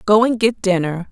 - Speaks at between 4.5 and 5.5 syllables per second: Yes, 5.1 syllables/s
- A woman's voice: Yes, female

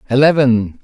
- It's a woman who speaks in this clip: No, male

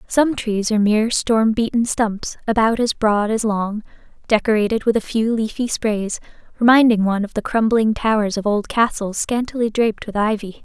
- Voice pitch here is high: Yes, high, 220 Hz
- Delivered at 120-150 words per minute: No, average, 175 wpm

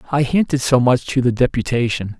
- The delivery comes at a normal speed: Yes, average, 190 wpm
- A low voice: Yes, low, 125 Hz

